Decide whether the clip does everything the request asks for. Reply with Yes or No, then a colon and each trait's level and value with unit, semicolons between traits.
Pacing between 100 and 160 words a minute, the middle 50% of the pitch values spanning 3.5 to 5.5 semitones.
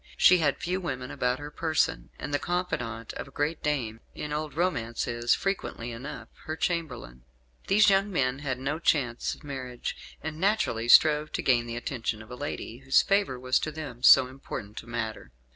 No: average, 190 wpm; average, 4.8 semitones